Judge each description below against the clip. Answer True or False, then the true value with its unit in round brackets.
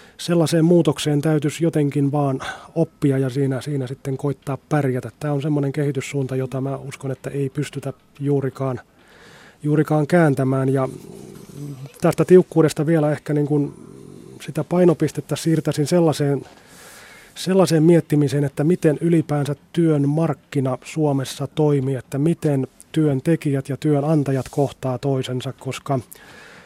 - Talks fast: False (120 wpm)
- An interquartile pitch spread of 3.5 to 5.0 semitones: False (2.6 semitones)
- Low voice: False (145 Hz)